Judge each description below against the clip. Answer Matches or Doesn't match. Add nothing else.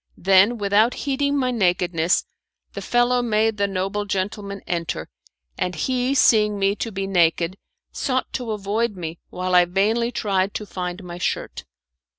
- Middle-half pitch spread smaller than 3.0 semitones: Doesn't match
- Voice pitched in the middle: Doesn't match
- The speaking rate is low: Doesn't match